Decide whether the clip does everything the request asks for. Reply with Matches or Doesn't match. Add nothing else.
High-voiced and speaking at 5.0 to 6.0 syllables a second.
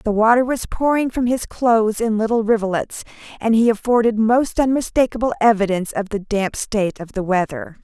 Matches